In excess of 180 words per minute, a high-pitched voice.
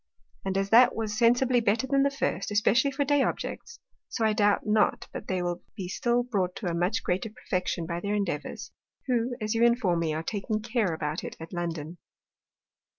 Yes: average, 200 wpm; high, 210 Hz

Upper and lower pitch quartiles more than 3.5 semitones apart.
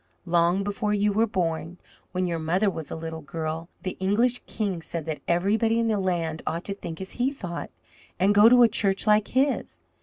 Yes: average, 4.1 semitones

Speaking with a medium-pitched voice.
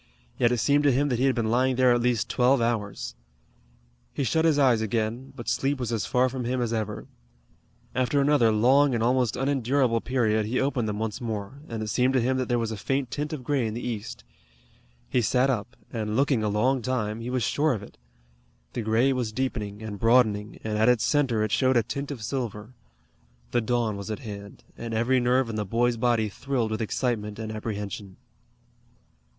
No: low, 120 Hz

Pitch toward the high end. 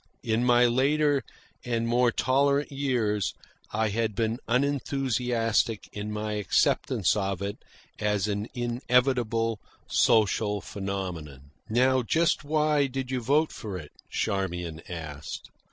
No: low, 115 Hz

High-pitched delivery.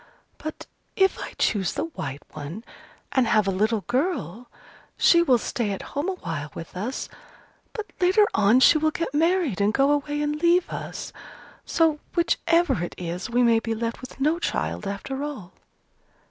Yes: very high, 260 Hz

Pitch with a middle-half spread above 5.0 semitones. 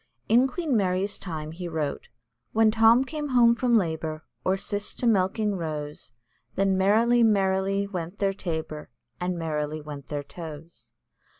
Yes: wide, 5.6 semitones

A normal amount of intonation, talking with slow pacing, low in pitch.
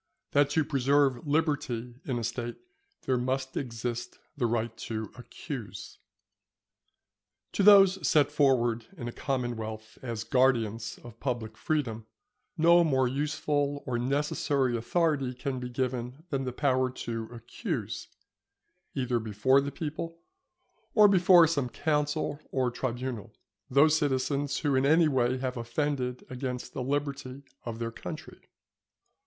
Yes: average, 3.3 semitones; slow, 130 wpm; low, 130 Hz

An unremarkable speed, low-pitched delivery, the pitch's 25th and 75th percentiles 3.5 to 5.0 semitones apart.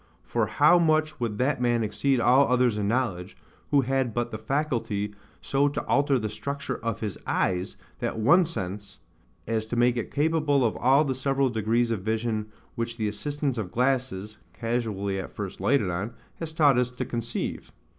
Yes: average, 180 wpm; low, 120 Hz; average, 4.3 semitones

